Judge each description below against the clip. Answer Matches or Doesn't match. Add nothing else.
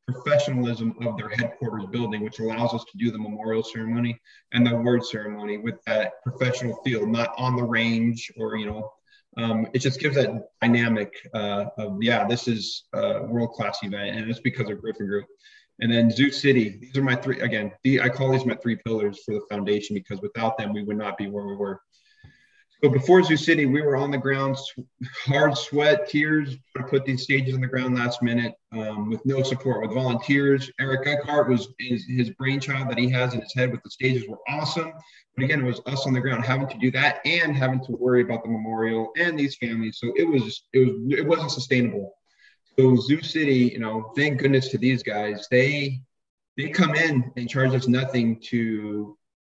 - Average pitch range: Matches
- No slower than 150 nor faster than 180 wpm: Doesn't match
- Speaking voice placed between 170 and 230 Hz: Doesn't match